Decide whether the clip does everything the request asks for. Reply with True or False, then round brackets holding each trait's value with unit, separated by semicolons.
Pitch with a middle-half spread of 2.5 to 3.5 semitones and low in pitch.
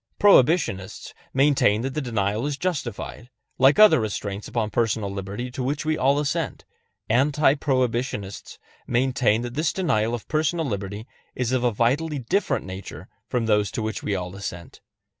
False (5.2 semitones; 120 Hz)